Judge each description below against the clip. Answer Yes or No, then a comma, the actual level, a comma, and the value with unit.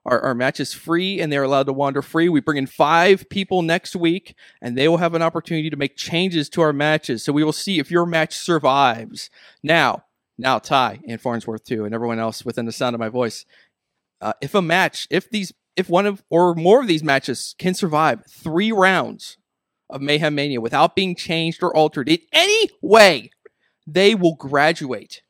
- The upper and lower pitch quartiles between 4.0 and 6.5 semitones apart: Yes, average, 4.4 semitones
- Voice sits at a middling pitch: Yes, medium, 160 Hz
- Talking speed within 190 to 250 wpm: Yes, average, 200 wpm